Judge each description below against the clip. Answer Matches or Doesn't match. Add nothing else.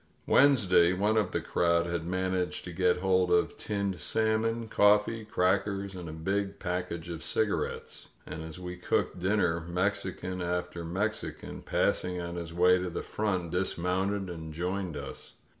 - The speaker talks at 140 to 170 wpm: Matches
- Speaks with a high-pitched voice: Doesn't match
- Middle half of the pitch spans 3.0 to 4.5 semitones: Doesn't match